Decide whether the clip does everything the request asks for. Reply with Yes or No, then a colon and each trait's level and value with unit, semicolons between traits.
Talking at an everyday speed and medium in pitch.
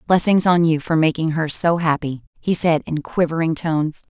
Yes: average, 190 wpm; medium, 165 Hz